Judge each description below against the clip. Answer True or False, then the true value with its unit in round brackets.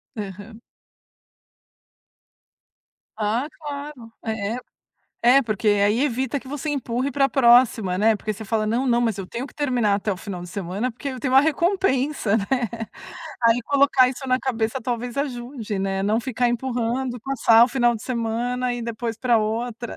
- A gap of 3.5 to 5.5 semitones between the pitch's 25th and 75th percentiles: False (3.1 semitones)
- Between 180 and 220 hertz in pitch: False (240 Hz)